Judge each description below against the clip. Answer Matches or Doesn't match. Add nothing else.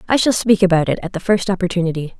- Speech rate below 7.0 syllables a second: Doesn't match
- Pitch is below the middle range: Doesn't match